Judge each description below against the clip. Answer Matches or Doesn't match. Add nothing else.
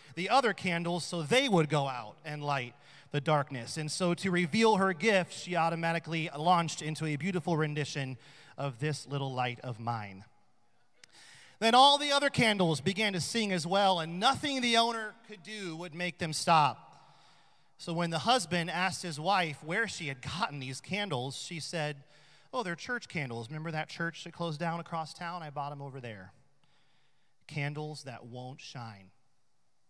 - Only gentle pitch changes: Doesn't match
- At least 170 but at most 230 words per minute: Matches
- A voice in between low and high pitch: Matches